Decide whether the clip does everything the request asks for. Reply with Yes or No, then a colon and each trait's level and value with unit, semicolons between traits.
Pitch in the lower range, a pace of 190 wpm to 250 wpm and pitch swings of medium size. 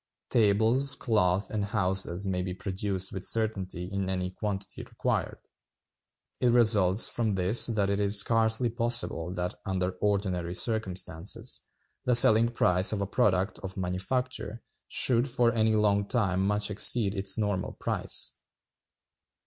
No: low, 100 Hz; slow, 135 wpm; average, 3.1 semitones